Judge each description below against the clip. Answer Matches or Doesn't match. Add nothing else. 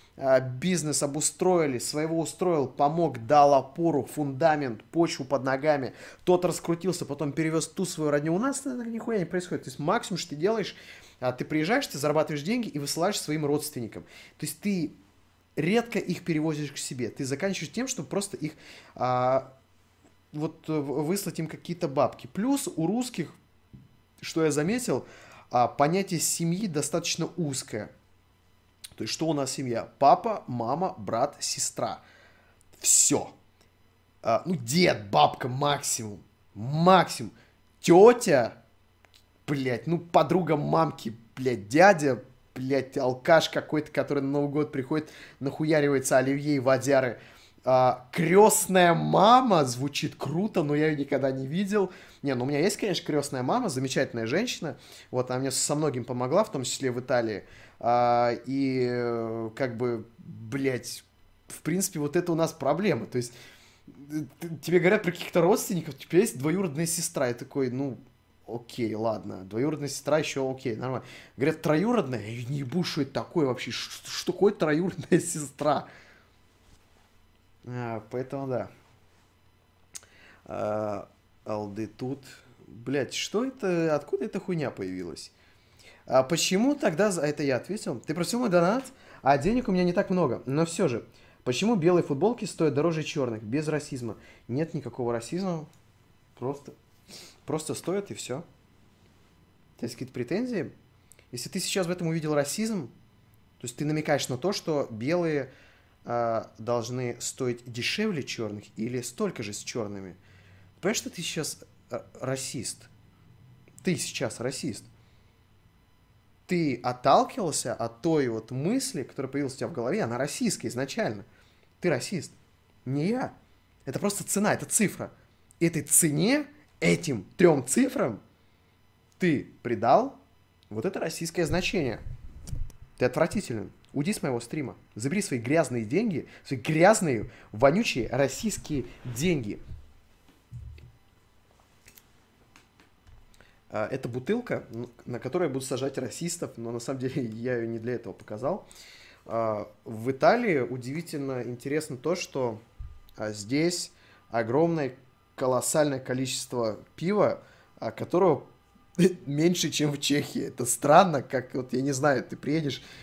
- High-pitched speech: Doesn't match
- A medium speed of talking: Matches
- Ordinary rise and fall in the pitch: Doesn't match